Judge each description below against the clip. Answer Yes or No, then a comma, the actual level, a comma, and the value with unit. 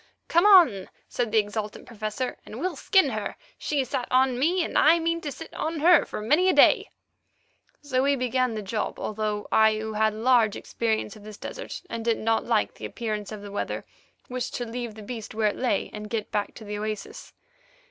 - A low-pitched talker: No, high, 225 Hz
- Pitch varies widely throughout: No, average, 3.7 semitones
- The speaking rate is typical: No, fast, 210 wpm